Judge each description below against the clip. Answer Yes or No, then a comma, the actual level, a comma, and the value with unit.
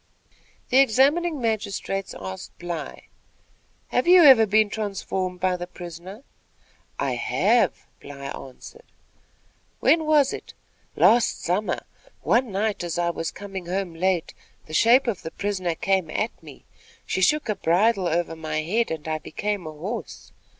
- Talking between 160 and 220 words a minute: No, average, 145 wpm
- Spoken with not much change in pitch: No, average, 4.8 semitones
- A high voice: Yes, high, 195 Hz